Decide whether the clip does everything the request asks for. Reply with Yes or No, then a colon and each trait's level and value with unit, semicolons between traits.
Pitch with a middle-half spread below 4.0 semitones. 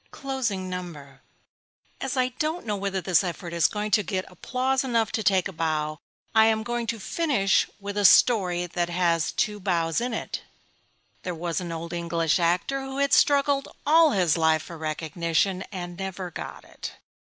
No: wide, 5.5 semitones